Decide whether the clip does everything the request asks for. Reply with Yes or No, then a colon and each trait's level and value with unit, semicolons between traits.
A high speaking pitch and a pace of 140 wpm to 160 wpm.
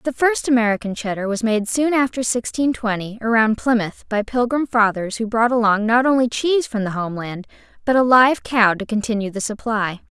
No: high, 230 Hz; average, 190 wpm